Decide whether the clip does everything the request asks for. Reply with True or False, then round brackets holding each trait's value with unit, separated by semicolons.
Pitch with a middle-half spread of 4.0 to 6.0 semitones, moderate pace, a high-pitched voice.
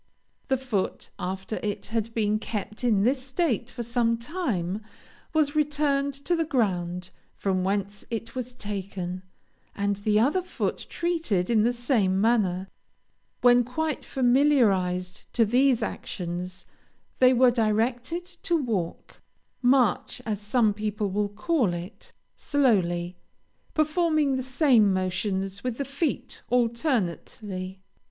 False (5.2 semitones; 125 wpm; 230 Hz)